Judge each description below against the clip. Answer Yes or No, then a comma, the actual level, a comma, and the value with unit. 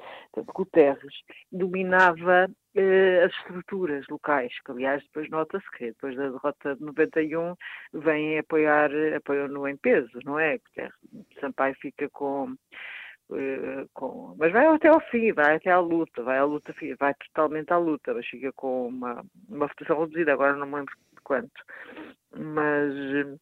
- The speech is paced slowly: No, average, 155 wpm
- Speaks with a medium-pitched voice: Yes, medium, 150 Hz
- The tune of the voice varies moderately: Yes, average, 3.7 semitones